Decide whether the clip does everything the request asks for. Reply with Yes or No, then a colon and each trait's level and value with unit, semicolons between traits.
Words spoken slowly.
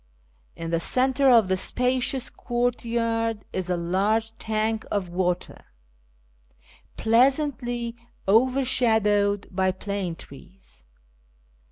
Yes: slow, 90 wpm